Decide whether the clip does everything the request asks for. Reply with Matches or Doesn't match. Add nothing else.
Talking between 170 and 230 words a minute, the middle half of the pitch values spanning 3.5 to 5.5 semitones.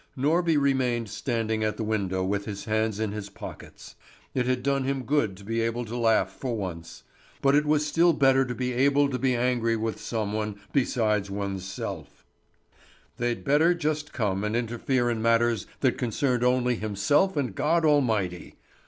Matches